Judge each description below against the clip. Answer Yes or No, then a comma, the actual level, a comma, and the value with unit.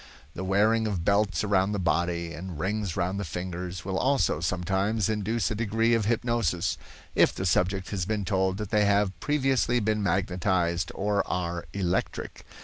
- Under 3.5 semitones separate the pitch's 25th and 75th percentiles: Yes, average, 3.0 semitones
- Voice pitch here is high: No, very low, 95 Hz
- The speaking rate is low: No, average, 165 wpm